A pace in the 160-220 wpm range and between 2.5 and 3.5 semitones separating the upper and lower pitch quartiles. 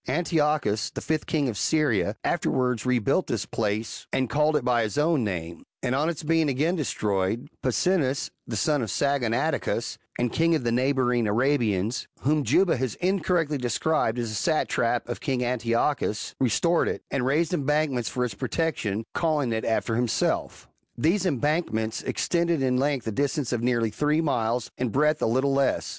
No: average, 170 wpm; average, 4.7 semitones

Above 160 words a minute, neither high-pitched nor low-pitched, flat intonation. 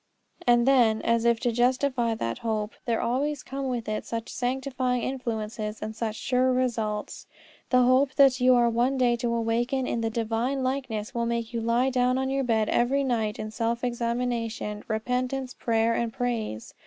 No: average, 180 wpm; high, 240 Hz; narrow, 2.1 semitones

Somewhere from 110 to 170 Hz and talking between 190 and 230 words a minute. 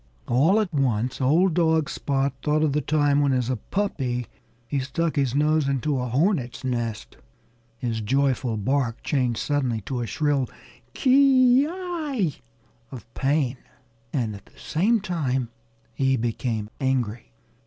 No: low, 135 Hz; average, 145 wpm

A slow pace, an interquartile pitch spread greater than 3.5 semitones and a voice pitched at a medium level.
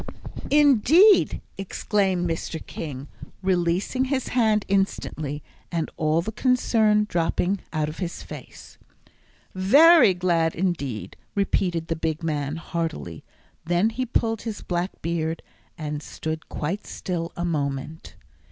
Yes: slow, 120 wpm; average, 4.7 semitones; medium, 175 Hz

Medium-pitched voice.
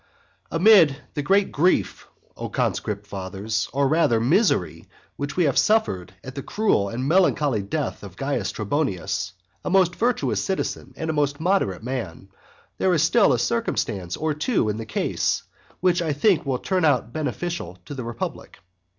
Yes: medium, 145 Hz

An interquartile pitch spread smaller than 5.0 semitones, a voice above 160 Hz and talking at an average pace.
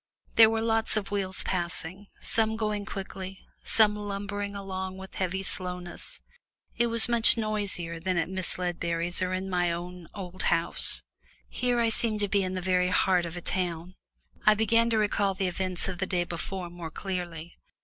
Yes: average, 2.7 semitones; high, 190 Hz; average, 180 wpm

